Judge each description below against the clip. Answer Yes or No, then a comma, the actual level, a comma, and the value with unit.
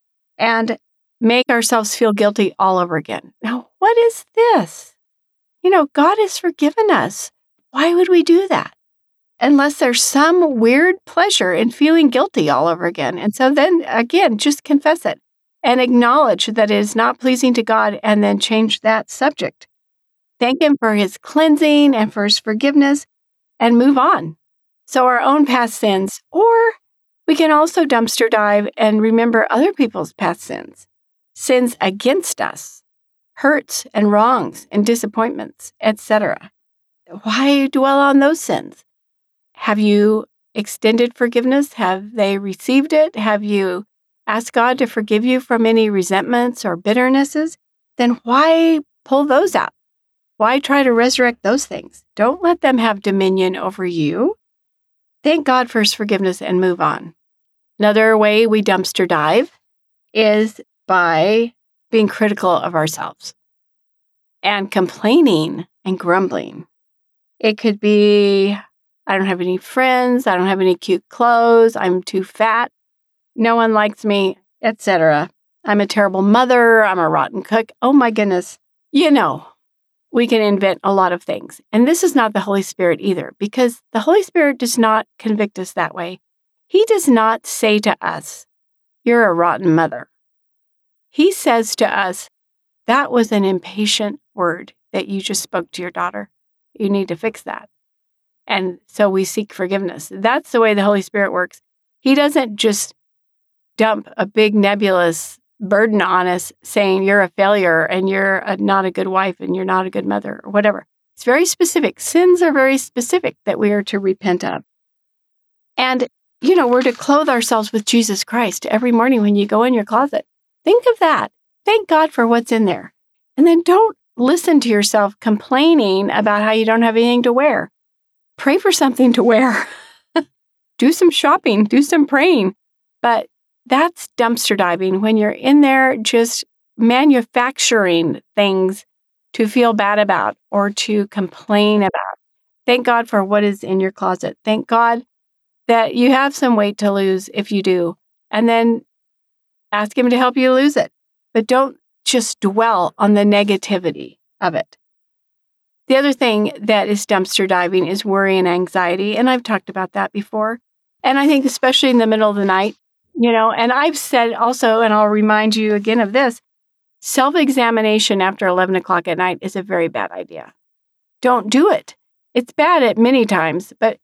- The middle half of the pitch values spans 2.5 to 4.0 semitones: No, average, 4.7 semitones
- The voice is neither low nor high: No, high, 225 Hz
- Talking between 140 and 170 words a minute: Yes, average, 165 wpm